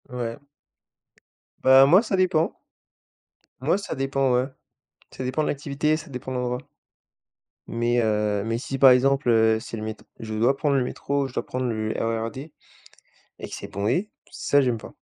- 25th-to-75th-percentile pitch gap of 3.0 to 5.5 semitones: Yes, average, 3.4 semitones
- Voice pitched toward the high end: No, low, 125 Hz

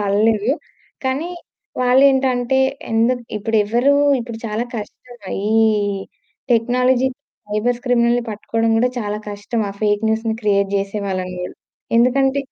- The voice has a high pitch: Yes, high, 230 Hz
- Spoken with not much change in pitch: No, average, 3.1 semitones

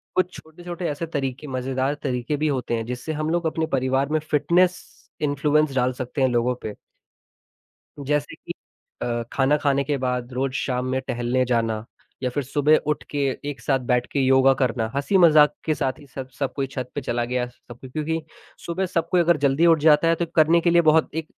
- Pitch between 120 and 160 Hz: Yes, medium, 140 Hz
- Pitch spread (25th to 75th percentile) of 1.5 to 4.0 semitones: Yes, average, 3.5 semitones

